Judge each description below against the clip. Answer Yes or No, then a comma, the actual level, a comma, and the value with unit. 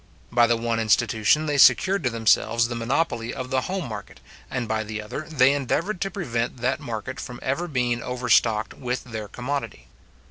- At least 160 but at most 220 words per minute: Yes, average, 180 wpm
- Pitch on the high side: No, low, 120 Hz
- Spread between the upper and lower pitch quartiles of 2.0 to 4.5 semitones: Yes, average, 3.4 semitones